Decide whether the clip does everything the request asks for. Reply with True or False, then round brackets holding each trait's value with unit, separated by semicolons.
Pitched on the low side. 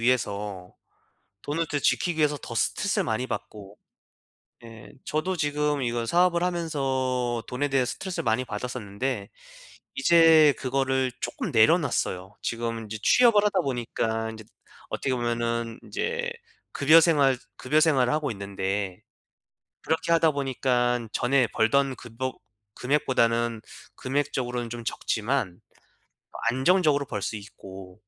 True (125 Hz)